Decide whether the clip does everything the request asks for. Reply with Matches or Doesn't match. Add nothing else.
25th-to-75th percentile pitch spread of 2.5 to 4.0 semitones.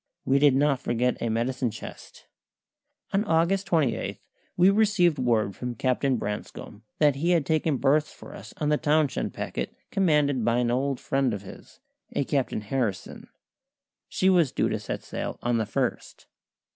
Doesn't match